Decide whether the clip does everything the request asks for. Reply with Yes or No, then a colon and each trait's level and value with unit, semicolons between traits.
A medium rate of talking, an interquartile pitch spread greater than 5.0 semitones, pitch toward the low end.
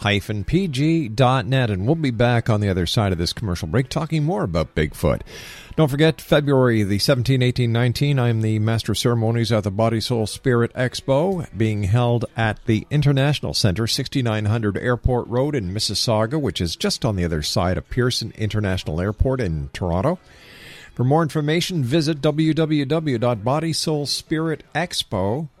Yes: average, 150 wpm; wide, 5.4 semitones; low, 120 Hz